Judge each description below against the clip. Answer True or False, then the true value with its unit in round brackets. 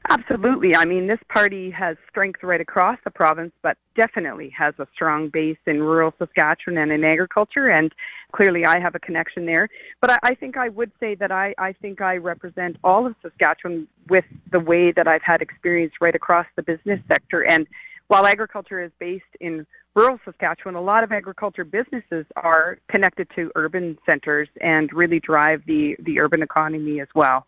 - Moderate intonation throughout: True (3.8 semitones)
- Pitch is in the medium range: True (175 Hz)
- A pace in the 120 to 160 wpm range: False (185 wpm)